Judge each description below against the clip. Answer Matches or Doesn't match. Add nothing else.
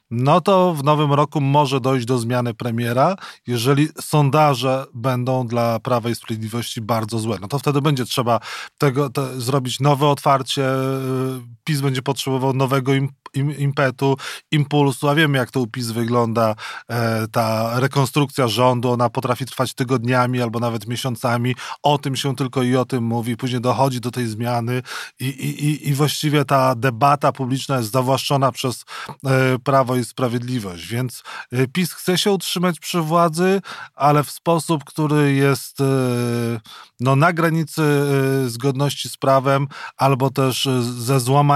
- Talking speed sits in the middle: Matches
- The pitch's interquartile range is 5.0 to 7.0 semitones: Doesn't match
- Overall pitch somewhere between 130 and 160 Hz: Matches